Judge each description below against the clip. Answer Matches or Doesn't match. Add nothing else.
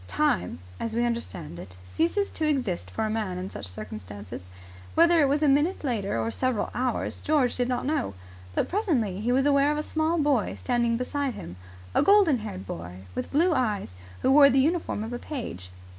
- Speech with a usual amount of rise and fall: Doesn't match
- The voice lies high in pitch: Matches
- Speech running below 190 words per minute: Doesn't match